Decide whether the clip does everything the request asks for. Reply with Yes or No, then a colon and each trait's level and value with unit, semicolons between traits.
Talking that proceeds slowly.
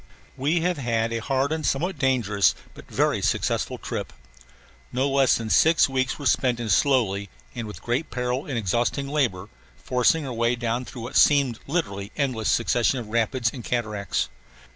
No: average, 170 wpm